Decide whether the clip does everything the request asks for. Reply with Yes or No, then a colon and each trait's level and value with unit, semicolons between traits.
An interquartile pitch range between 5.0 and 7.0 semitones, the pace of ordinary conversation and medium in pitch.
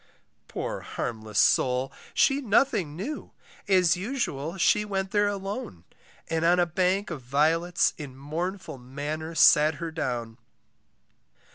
No: wide, 5.5 semitones; slow, 125 wpm; medium, 165 Hz